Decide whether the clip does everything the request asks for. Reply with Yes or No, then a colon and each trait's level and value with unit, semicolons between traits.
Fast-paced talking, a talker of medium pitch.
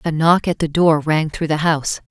Yes: fast, 255 wpm; medium, 160 Hz